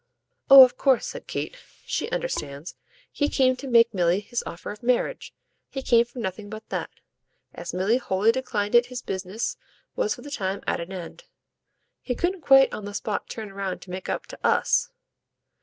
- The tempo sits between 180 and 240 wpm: Yes, average, 190 wpm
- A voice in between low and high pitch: No, high, 230 Hz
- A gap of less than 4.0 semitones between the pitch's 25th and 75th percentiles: No, average, 5.3 semitones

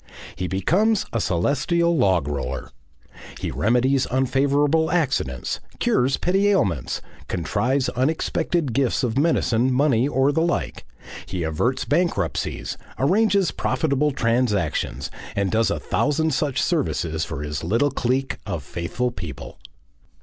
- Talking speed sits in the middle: No, slow, 120 wpm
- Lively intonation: Yes, wide, 7.6 semitones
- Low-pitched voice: Yes, low, 130 Hz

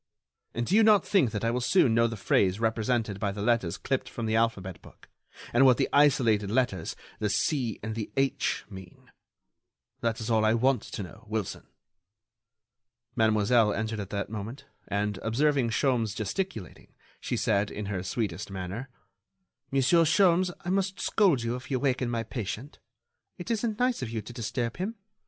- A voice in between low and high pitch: No, low, 115 Hz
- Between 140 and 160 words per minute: No, average, 170 wpm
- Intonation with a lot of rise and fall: No, average, 4.3 semitones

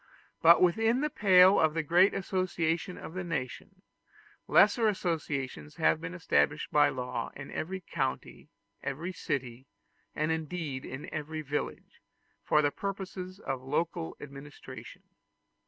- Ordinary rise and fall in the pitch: Yes, average, 4.3 semitones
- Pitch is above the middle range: No, medium, 160 Hz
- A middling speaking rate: No, slow, 130 wpm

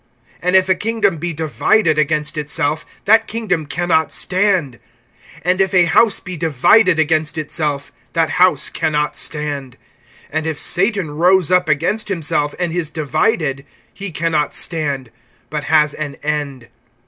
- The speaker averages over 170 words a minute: No, average, 155 wpm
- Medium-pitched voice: Yes, medium, 160 Hz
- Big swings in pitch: No, average, 3.5 semitones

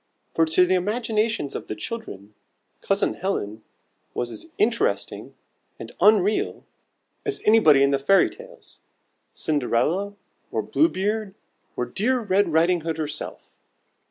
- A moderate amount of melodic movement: No, wide, 6.4 semitones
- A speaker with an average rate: No, slow, 130 wpm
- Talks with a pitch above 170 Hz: Yes, high, 190 Hz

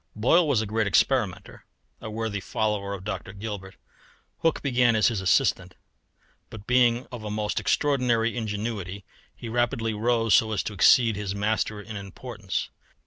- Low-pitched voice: Yes, low, 110 Hz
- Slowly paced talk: No, average, 155 wpm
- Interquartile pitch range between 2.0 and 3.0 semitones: Yes, narrow, 2.6 semitones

